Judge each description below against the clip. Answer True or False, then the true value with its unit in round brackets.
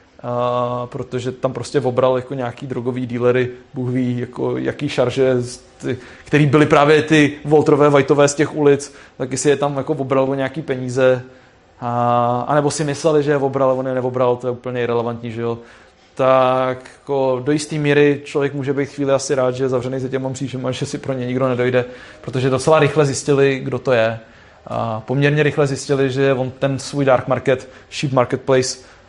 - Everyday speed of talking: False (190 wpm)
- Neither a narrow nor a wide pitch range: False (2.2 semitones)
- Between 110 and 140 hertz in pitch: True (130 Hz)